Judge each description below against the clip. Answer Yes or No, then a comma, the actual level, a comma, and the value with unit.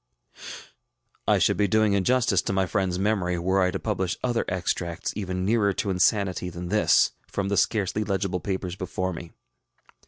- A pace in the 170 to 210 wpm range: Yes, average, 175 wpm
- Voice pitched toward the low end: Yes, very low, 95 Hz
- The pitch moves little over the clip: Yes, narrow, 2.2 semitones